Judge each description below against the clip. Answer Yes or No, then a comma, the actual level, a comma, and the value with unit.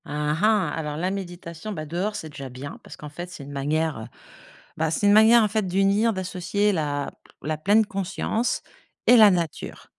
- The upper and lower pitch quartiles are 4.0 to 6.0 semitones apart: Yes, average, 5.2 semitones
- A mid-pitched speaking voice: Yes, medium, 175 Hz